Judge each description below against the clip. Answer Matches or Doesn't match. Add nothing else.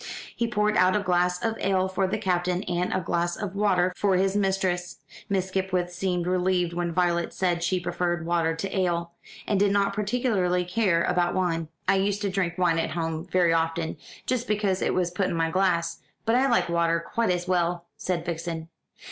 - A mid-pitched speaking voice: Matches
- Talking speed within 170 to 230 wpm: Matches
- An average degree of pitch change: Doesn't match